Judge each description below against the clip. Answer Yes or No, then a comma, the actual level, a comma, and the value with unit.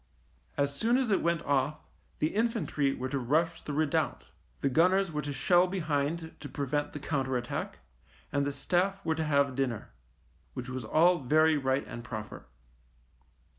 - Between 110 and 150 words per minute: No, average, 180 wpm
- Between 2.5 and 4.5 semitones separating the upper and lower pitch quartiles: Yes, average, 3.8 semitones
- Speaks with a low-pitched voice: No, medium, 145 Hz